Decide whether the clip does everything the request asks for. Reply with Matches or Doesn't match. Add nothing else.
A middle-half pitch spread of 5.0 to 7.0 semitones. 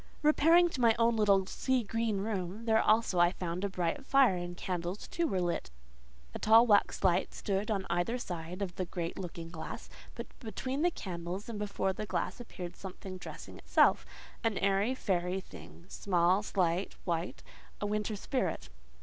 Doesn't match